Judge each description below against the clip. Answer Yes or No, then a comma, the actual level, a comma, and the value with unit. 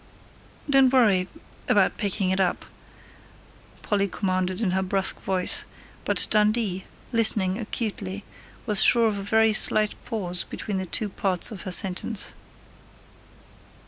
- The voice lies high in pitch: Yes, high, 200 Hz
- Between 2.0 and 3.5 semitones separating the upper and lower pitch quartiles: Yes, average, 2.7 semitones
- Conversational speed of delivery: No, slow, 130 wpm